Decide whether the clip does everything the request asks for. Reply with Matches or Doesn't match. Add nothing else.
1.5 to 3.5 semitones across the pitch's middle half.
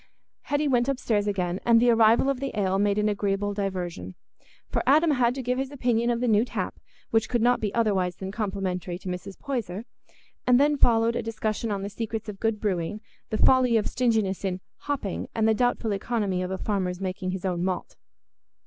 Doesn't match